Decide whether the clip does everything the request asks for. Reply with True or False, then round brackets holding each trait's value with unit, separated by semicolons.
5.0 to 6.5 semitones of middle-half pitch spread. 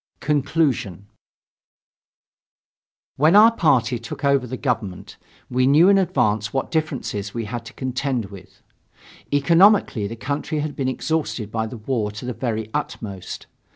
True (5.3 semitones)